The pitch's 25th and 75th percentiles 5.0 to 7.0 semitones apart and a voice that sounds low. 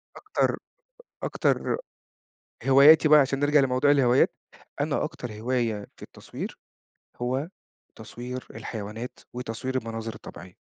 No: average, 3.7 semitones; low, 125 Hz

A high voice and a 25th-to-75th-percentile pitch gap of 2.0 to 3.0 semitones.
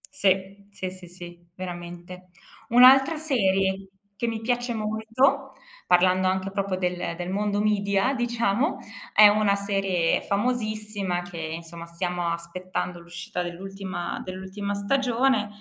No: high, 195 Hz; average, 3.4 semitones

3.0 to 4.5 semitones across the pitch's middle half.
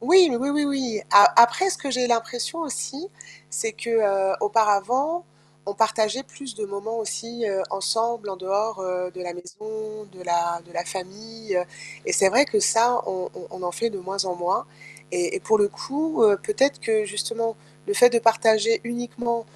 Yes: average, 3.7 semitones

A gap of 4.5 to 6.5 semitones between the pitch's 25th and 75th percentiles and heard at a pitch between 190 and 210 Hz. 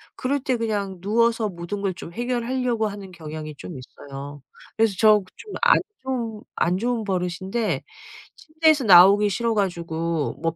Yes: average, 5.3 semitones; high, 205 Hz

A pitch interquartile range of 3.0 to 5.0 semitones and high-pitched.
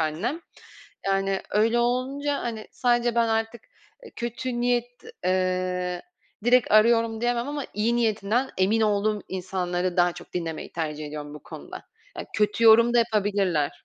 Yes: average, 4.6 semitones; high, 215 Hz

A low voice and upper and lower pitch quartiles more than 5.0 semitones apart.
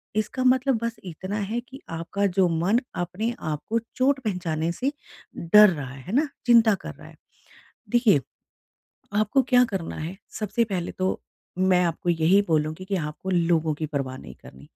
No: medium, 185 Hz; wide, 5.5 semitones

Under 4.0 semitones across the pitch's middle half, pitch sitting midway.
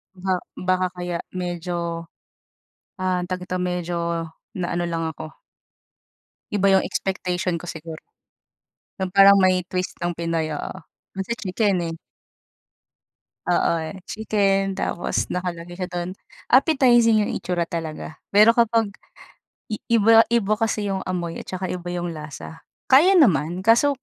Yes: average, 2.9 semitones; medium, 180 Hz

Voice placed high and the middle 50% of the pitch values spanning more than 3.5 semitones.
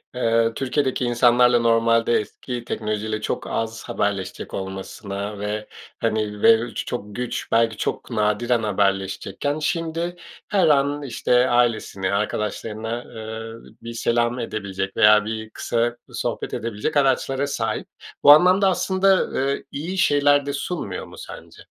No: low, 115 Hz; average, 4.1 semitones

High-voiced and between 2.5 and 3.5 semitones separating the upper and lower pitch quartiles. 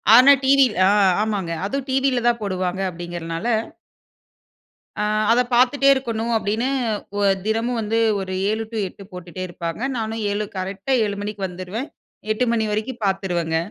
No: high, 215 Hz; average, 4.3 semitones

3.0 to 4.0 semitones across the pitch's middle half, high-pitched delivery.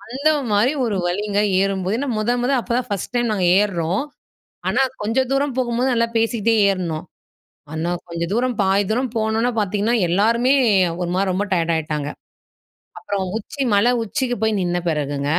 No: average, 4.7 semitones; high, 210 Hz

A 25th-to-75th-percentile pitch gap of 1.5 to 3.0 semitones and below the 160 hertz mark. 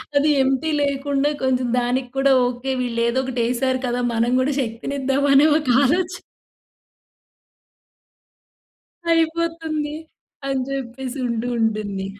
No: average, 2.7 semitones; very high, 265 Hz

